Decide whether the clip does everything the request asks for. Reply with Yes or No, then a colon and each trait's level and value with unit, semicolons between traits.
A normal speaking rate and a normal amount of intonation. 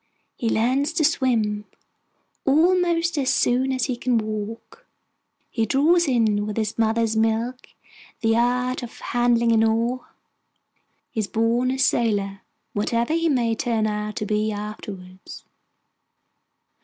No: slow, 130 wpm; average, 3.0 semitones